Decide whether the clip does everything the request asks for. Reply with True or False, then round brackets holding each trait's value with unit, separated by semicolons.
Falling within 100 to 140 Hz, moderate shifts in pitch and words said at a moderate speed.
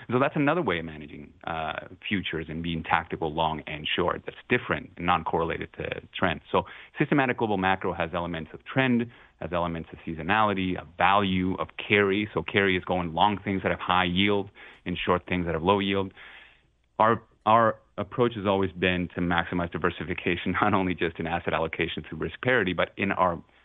False (90 Hz; 3.0 semitones; 190 wpm)